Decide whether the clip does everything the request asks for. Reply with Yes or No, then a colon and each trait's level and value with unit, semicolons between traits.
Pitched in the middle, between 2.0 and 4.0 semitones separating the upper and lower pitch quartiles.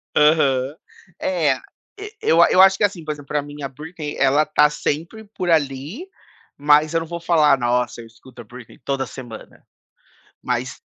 Yes: medium, 150 Hz; average, 3.7 semitones